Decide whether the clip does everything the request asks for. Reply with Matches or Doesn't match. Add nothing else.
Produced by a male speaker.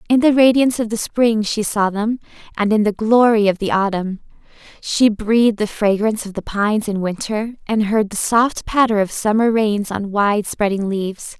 Doesn't match